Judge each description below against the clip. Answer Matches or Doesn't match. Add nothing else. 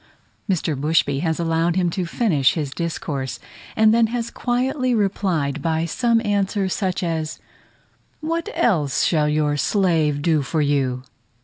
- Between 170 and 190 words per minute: Doesn't match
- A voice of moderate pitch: Matches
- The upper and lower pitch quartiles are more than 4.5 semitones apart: Matches